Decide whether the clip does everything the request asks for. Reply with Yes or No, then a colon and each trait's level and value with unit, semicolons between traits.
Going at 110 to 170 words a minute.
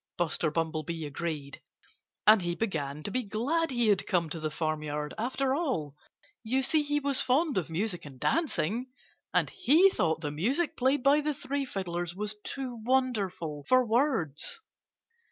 Yes: average, 160 wpm